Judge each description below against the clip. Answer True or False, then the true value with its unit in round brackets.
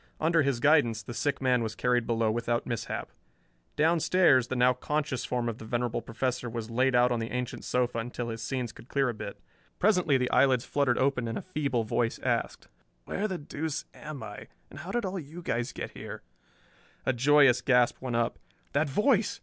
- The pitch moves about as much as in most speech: True (3.8 semitones)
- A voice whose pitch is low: True (125 Hz)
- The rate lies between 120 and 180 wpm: False (200 wpm)